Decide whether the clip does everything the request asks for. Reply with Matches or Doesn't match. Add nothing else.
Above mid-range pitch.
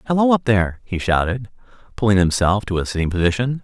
Doesn't match